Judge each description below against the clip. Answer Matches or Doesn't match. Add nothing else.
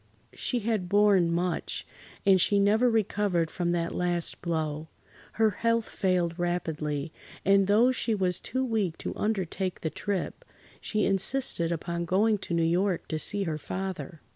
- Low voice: Doesn't match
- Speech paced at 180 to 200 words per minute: Doesn't match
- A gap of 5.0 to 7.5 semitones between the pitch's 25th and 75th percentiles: Doesn't match